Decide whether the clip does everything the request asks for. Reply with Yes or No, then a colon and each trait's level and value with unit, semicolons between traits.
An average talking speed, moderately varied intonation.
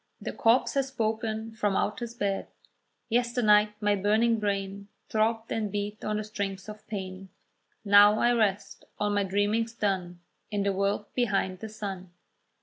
No: average, 155 wpm; narrow, 2.0 semitones